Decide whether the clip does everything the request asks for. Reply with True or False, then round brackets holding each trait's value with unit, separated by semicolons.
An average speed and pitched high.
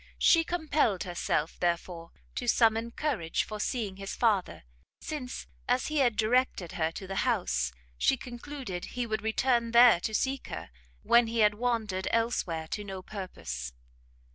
True (155 wpm; 220 Hz)